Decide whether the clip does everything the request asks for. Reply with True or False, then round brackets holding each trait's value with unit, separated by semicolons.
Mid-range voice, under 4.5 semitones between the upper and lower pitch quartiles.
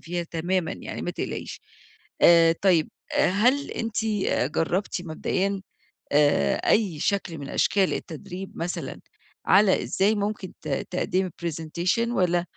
True (180 Hz; 3.2 semitones)